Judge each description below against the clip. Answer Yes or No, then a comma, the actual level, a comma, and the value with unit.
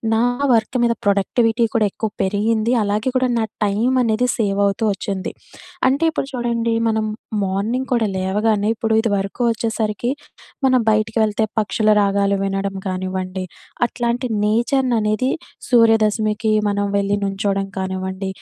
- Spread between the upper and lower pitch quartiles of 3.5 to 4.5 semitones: No, average, 2.7 semitones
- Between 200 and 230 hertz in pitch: Yes, high, 215 Hz